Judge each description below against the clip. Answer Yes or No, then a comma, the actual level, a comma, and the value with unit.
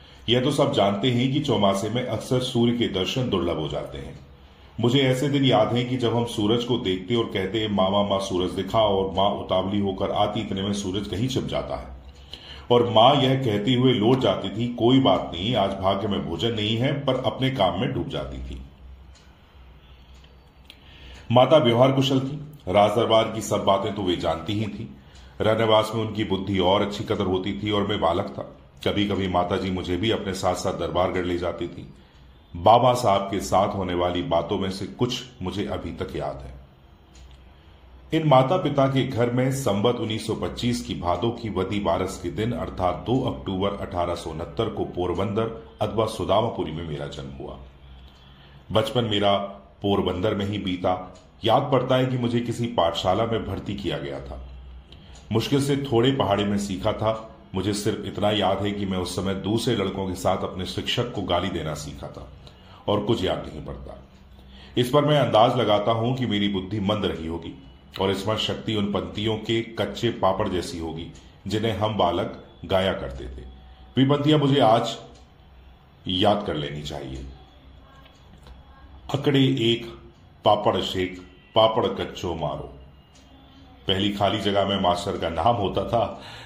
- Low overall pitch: Yes, low, 100 Hz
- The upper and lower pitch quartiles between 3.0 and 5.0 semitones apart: No, wide, 5.4 semitones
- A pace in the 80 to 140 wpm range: No, average, 175 wpm